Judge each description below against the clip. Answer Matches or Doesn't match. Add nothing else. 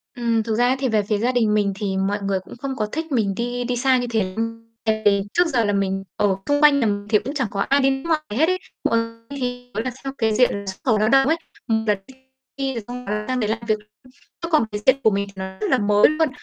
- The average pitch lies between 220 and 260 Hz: Matches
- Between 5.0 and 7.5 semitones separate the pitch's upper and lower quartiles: Doesn't match